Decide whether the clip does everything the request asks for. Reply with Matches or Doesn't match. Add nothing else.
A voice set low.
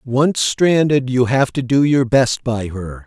Matches